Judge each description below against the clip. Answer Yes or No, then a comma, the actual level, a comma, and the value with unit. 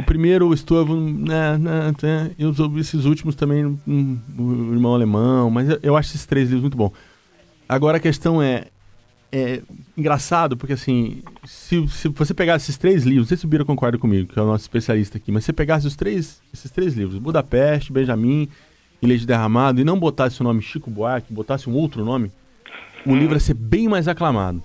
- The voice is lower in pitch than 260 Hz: Yes, medium, 140 Hz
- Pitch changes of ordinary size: Yes, average, 4.4 semitones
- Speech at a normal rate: No, fast, 205 wpm